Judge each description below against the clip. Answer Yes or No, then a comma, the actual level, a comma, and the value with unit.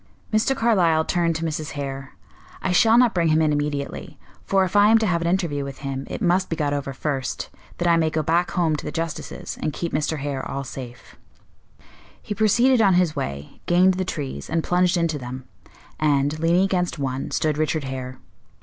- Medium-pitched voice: Yes, medium, 160 Hz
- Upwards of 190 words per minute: Yes, fast, 205 wpm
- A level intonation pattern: No, average, 4.2 semitones